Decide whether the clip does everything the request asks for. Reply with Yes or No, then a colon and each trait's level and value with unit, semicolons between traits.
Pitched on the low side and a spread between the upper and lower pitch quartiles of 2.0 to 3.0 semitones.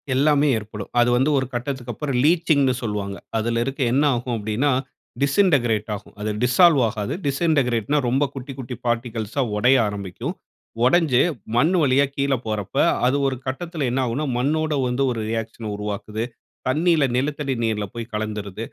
No: low, 125 Hz; average, 4.3 semitones